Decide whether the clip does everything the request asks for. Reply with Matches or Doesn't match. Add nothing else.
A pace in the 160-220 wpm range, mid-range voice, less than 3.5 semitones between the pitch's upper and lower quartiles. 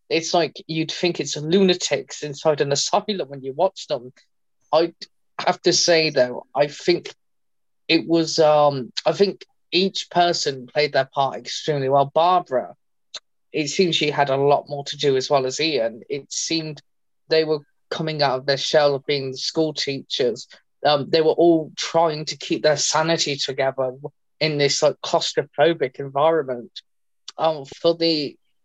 Matches